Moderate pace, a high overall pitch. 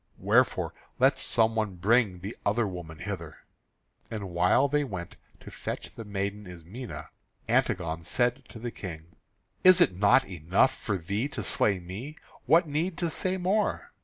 No: average, 160 wpm; low, 105 Hz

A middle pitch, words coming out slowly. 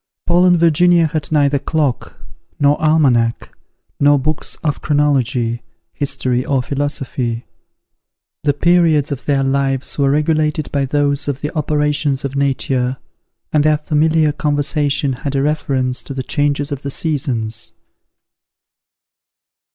Yes: medium, 145 Hz; slow, 130 wpm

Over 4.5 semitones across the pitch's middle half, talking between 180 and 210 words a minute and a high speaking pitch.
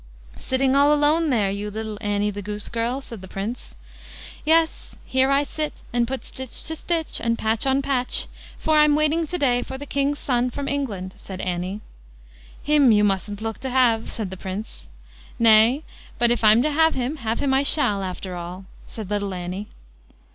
Yes: average, 5.3 semitones; average, 190 wpm; high, 240 Hz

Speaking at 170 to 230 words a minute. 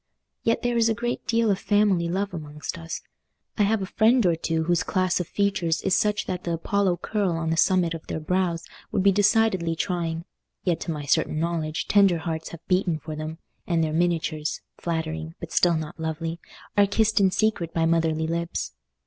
Yes: average, 190 wpm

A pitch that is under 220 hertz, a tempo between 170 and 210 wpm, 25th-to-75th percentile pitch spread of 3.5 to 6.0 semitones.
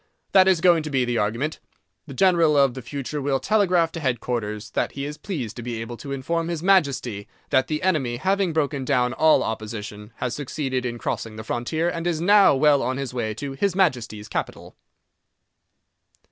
Yes: medium, 140 Hz; average, 190 wpm; wide, 5.5 semitones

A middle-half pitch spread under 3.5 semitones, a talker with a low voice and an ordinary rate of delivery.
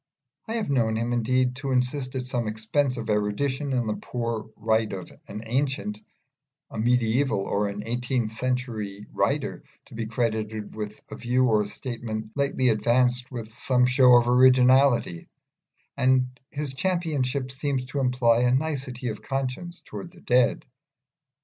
Yes: average, 2.9 semitones; low, 125 Hz; average, 150 wpm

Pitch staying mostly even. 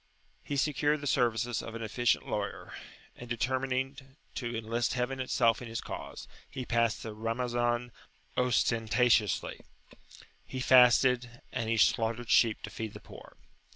Yes: narrow, 2.0 semitones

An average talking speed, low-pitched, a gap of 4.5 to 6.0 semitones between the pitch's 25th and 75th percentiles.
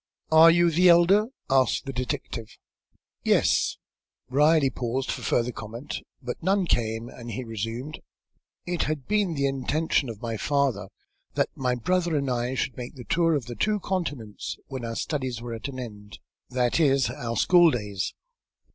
Yes: average, 165 wpm; low, 130 Hz; average, 5.3 semitones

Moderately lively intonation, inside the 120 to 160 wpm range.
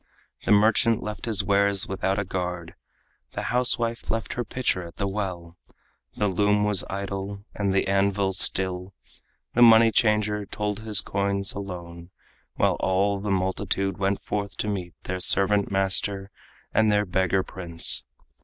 No: narrow, 1.7 semitones; average, 150 wpm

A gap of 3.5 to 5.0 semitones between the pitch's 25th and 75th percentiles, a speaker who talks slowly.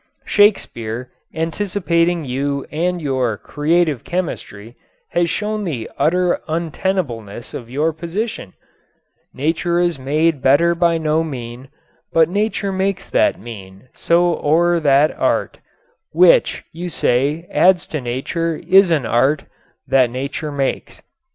Yes: average, 4.7 semitones; slow, 120 wpm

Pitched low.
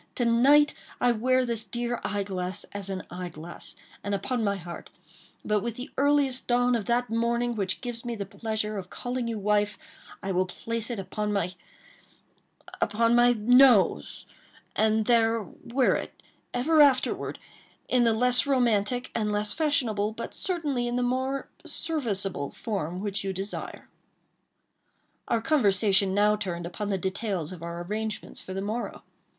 No: high, 220 Hz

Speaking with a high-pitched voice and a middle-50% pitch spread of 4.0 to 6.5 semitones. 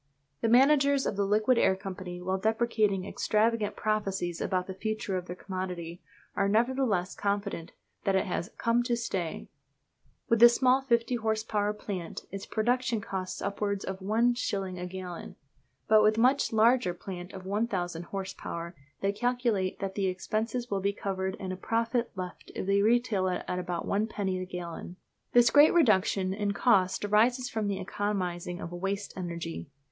No: high, 200 Hz; average, 3.5 semitones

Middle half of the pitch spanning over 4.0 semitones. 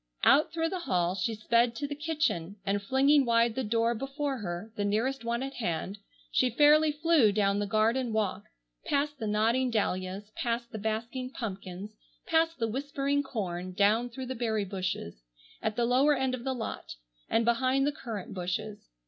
Yes: average, 4.6 semitones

